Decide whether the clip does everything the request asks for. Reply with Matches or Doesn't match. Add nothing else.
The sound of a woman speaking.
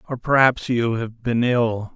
Doesn't match